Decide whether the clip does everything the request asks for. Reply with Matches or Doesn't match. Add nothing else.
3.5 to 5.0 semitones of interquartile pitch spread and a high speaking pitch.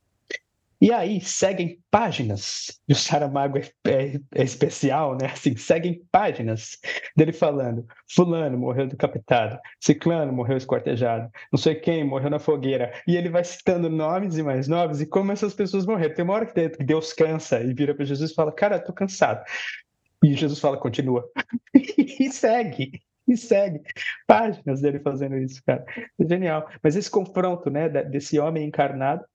Doesn't match